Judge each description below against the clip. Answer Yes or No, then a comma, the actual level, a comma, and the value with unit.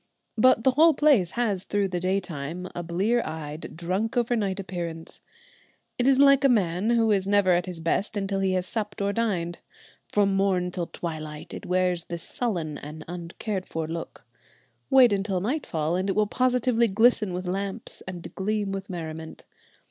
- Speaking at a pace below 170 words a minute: No, average, 180 wpm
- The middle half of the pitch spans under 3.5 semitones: No, average, 4.1 semitones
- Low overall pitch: No, high, 190 Hz